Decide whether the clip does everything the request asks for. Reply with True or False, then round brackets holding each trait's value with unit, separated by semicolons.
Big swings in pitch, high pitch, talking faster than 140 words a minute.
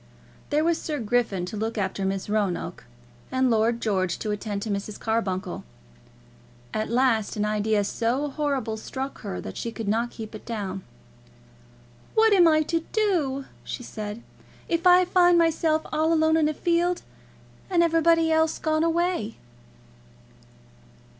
True (7.3 semitones; 245 Hz; 150 wpm)